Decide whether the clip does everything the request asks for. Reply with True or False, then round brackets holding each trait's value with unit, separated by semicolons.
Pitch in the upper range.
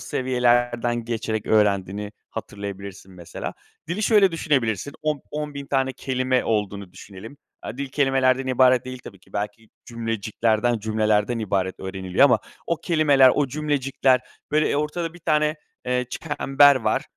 False (125 Hz)